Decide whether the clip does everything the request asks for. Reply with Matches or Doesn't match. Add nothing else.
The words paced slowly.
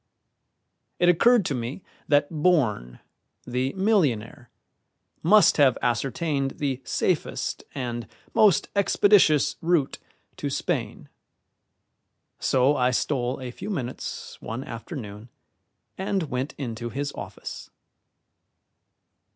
Matches